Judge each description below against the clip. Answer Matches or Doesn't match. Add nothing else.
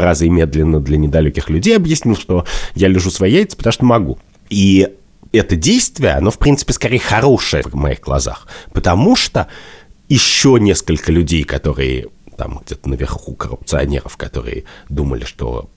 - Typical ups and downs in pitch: Doesn't match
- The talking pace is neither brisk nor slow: Matches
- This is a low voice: Matches